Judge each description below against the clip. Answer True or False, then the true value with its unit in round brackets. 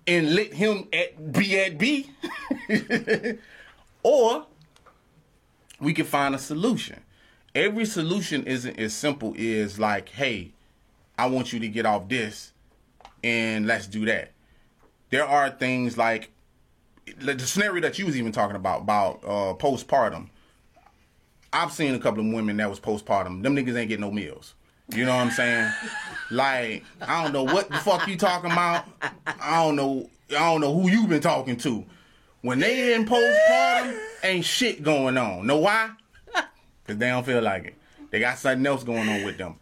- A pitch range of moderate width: False (8.9 semitones)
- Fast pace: False (175 wpm)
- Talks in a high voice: False (140 Hz)